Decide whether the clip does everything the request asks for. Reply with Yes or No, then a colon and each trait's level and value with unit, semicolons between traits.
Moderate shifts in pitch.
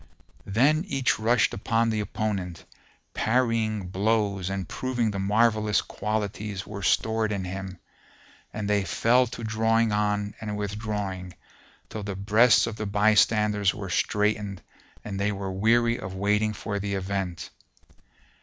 No: narrow, 2.1 semitones